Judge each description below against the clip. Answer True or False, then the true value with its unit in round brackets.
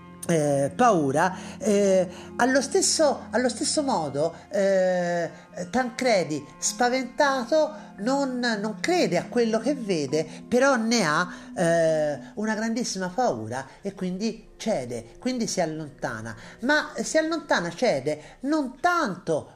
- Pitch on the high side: True (215 Hz)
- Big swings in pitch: True (6.7 semitones)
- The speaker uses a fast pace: False (115 wpm)